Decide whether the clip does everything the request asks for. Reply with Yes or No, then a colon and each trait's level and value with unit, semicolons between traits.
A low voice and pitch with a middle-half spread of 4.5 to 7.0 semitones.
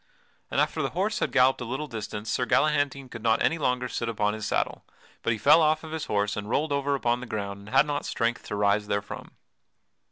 Yes: low, 125 Hz; average, 5.2 semitones